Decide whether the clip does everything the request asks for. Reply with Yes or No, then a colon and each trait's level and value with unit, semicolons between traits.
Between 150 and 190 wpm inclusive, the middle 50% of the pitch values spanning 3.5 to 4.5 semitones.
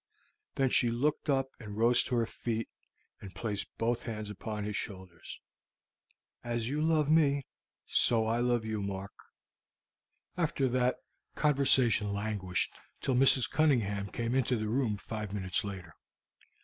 No: average, 140 wpm; average, 4.2 semitones